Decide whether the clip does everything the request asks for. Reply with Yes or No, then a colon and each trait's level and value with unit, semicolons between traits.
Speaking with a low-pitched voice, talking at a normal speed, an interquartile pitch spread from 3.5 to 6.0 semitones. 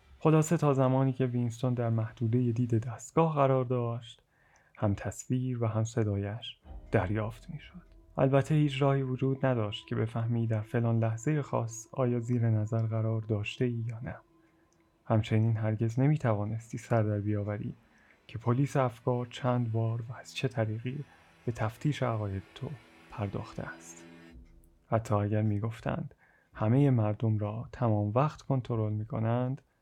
No: low, 115 Hz; average, 145 wpm; average, 3.1 semitones